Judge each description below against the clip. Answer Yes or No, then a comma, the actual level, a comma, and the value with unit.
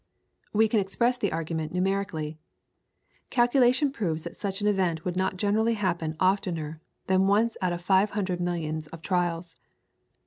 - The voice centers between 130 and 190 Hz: Yes, medium, 185 Hz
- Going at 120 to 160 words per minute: Yes, average, 150 wpm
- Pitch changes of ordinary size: Yes, average, 3.7 semitones